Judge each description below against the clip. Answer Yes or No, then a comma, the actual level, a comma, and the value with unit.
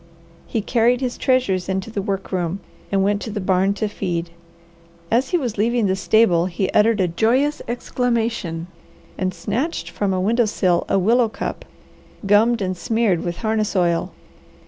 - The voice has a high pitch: Yes, high, 205 Hz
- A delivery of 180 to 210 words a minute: No, average, 170 wpm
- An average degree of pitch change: Yes, average, 3.8 semitones